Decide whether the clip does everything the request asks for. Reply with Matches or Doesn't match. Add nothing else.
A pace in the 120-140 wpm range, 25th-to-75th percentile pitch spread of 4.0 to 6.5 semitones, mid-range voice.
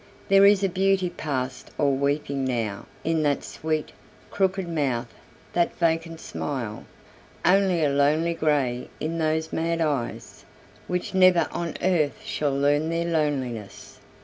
Doesn't match